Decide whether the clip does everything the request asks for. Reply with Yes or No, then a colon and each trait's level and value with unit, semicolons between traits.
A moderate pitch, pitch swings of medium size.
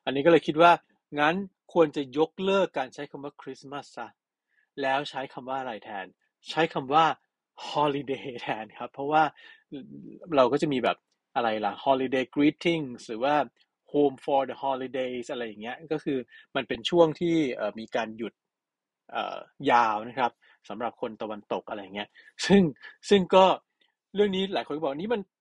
Yes: medium, 145 Hz; average, 4.2 semitones